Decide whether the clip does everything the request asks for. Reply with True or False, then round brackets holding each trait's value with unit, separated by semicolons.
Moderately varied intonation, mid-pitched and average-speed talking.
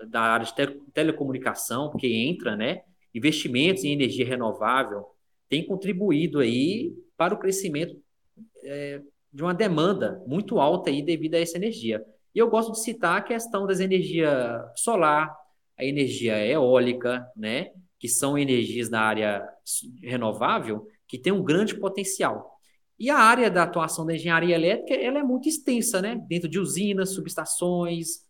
False (7.2 semitones; 165 Hz; 150 wpm)